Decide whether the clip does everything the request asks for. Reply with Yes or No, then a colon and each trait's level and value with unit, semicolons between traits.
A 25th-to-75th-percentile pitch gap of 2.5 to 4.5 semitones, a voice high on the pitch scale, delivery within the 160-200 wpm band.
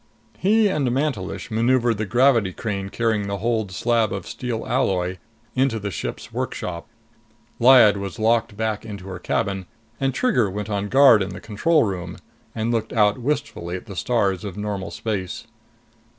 No: average, 3.6 semitones; low, 110 Hz; average, 165 wpm